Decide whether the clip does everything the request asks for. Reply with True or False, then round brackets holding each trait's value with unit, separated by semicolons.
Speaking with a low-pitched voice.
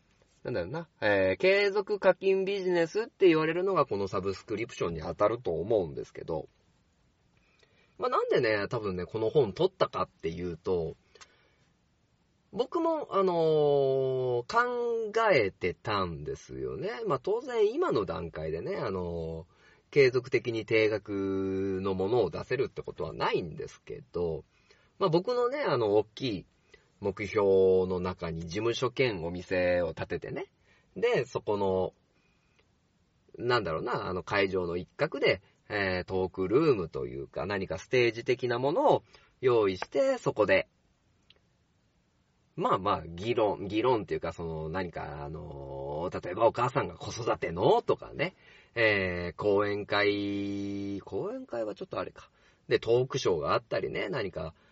True (110 Hz)